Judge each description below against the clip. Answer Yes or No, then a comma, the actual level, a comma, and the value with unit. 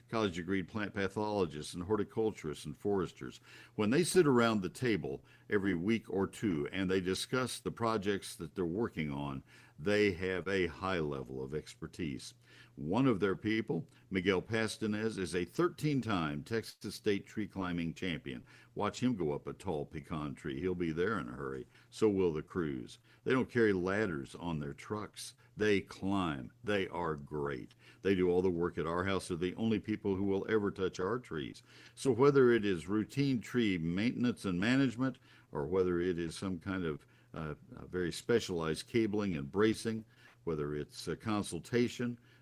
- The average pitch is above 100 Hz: No, very low, 95 Hz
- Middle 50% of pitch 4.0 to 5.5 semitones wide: Yes, average, 4.4 semitones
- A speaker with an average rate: Yes, average, 175 wpm